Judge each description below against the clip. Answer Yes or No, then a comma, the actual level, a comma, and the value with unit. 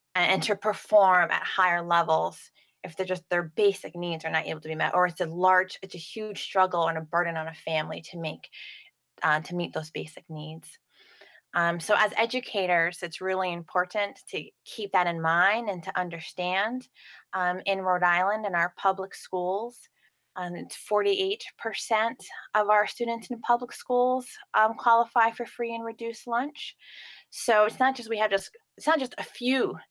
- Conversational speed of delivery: Yes, average, 185 wpm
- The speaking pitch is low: No, high, 190 Hz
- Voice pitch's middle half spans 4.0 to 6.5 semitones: Yes, average, 4.5 semitones